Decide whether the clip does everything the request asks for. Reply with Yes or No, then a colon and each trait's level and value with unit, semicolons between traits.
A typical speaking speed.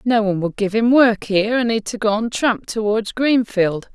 No: fast, 230 wpm